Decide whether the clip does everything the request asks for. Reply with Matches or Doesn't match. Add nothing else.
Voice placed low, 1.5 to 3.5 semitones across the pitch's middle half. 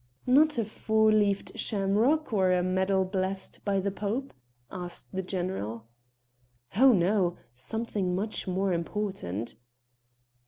Doesn't match